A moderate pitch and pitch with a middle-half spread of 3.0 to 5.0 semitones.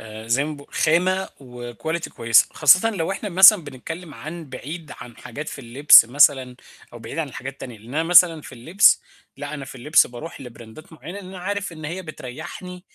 No: medium, 150 Hz; wide, 5.5 semitones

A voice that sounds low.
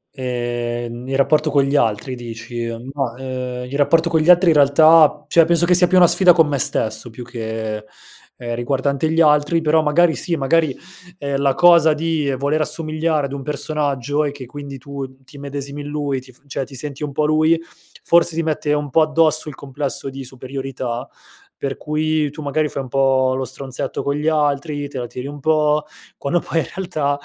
No: medium, 145 Hz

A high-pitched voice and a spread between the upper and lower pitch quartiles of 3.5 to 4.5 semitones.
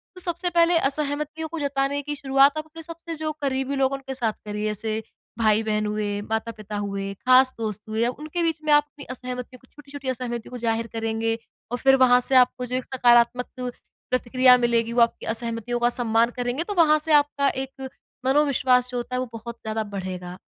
Yes: very high, 250 Hz; average, 4.0 semitones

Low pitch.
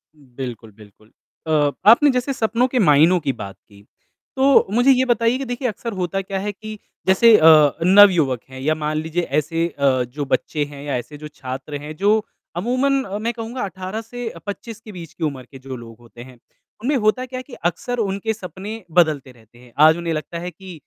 No: medium, 175 Hz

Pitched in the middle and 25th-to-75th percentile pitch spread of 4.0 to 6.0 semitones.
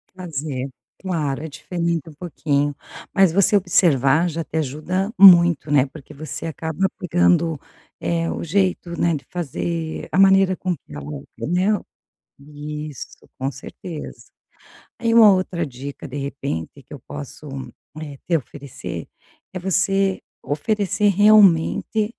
Yes: medium, 165 Hz; average, 4.3 semitones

